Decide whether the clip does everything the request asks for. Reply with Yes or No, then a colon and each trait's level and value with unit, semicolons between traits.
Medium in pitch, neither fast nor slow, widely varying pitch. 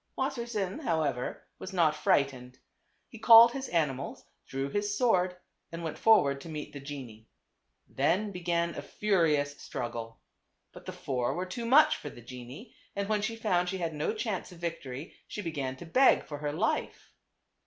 Yes: medium, 170 Hz; average, 175 wpm; wide, 6.9 semitones